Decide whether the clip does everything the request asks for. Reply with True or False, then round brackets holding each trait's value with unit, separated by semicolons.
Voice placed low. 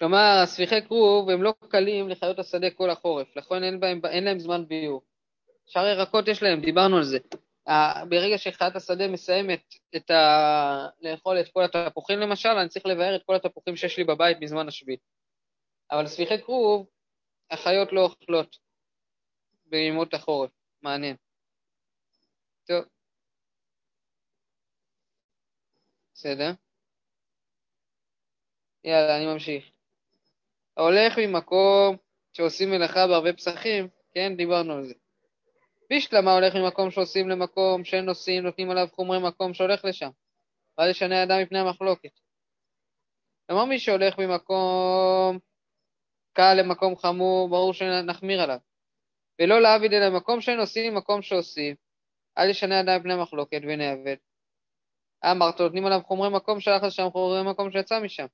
False (185 Hz)